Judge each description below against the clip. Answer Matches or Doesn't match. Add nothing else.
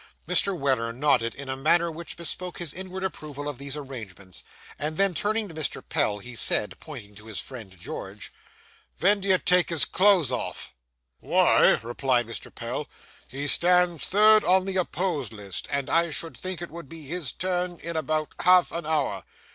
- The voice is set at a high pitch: Doesn't match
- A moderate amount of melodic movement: Doesn't match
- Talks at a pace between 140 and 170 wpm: Doesn't match